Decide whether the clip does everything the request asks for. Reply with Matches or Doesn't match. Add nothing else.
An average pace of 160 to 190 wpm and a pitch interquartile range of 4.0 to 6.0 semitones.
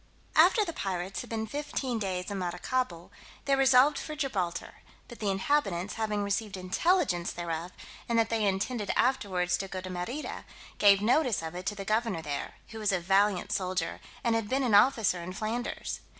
Matches